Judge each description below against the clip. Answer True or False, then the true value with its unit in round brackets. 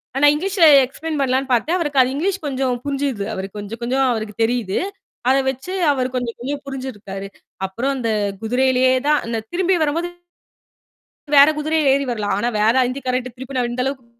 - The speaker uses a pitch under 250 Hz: False (260 Hz)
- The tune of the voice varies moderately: True (3.5 semitones)